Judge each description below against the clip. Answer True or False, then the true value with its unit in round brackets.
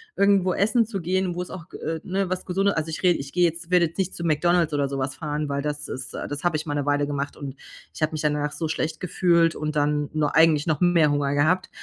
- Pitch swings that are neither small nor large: True (3.5 semitones)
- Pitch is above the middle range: False (160 Hz)